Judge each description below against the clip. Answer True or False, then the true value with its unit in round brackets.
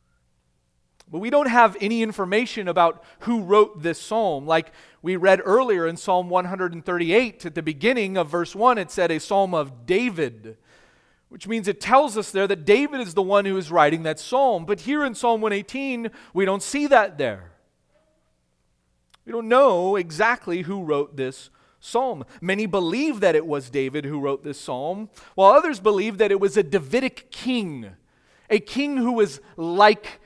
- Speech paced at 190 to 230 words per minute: False (175 wpm)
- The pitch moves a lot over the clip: True (5.8 semitones)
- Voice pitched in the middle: False (195 Hz)